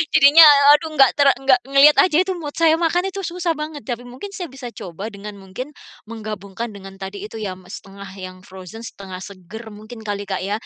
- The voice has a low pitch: No, high, 225 Hz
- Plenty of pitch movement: Yes, wide, 7.1 semitones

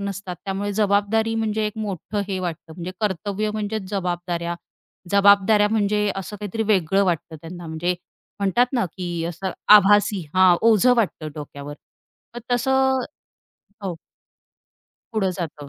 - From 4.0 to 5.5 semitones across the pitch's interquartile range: No, average, 3.3 semitones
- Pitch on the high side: Yes, high, 200 Hz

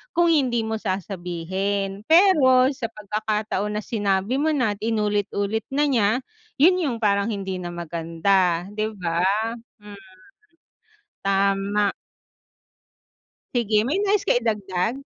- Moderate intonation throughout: Yes, average, 3.9 semitones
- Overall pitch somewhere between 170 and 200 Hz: No, high, 210 Hz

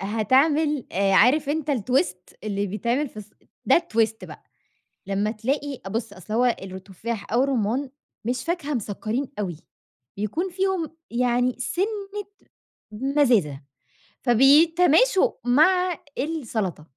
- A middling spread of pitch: No, wide, 6.6 semitones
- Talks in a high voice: Yes, very high, 250 Hz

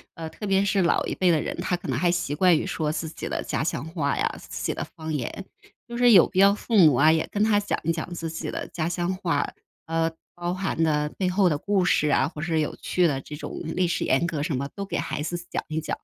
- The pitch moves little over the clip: No, average, 3.1 semitones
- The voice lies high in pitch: No, medium, 165 Hz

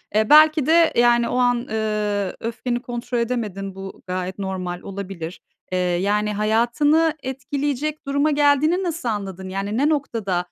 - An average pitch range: No, wide, 6.4 semitones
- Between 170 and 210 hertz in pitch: No, high, 235 Hz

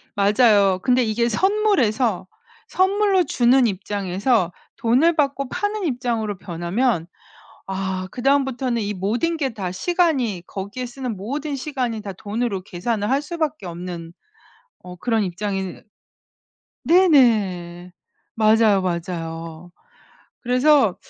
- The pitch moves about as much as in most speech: No, wide, 6.1 semitones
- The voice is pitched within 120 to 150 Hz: No, high, 225 Hz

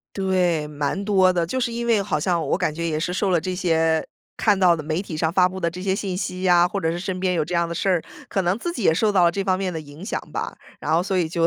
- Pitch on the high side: No, medium, 180 Hz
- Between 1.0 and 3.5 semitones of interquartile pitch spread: Yes, narrow, 2.6 semitones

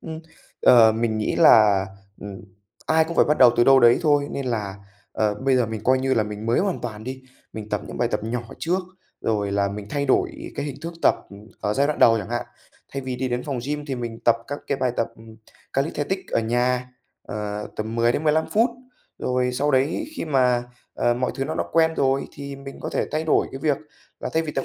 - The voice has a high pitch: No, low, 125 Hz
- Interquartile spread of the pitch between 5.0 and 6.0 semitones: No, average, 4.1 semitones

